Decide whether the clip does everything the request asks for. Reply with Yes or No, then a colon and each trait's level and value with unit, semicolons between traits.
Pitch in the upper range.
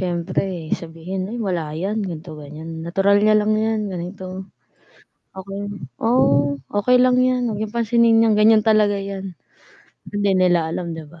Yes: high, 195 Hz